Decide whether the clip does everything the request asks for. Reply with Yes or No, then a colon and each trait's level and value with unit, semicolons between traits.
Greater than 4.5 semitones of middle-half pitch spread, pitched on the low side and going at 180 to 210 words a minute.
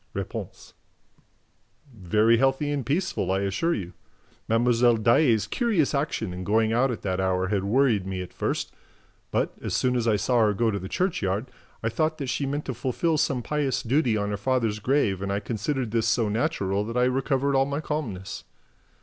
Yes: average, 5.0 semitones; low, 115 Hz; average, 190 wpm